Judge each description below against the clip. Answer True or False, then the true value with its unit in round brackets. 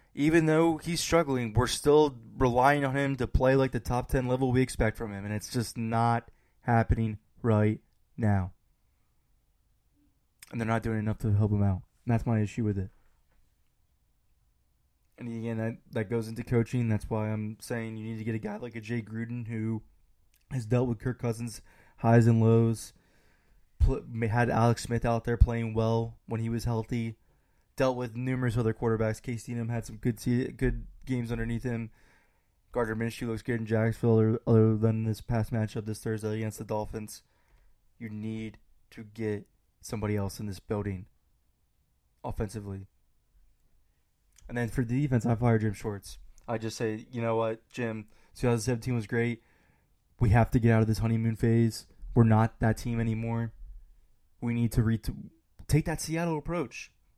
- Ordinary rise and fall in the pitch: False (1.8 semitones)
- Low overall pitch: True (115 Hz)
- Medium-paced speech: True (175 wpm)